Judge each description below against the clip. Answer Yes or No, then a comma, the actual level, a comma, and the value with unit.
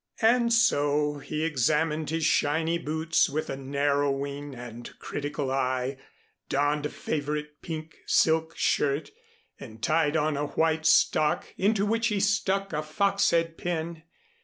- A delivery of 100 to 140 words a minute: Yes, slow, 135 wpm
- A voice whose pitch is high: No, medium, 155 Hz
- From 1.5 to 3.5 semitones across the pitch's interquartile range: Yes, narrow, 2.4 semitones